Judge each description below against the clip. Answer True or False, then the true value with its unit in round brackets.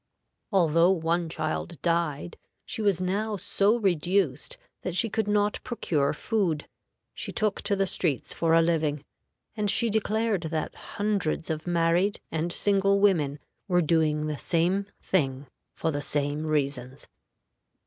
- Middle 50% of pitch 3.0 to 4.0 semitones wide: False (4.6 semitones)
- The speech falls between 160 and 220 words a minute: False (140 wpm)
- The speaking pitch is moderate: True (170 Hz)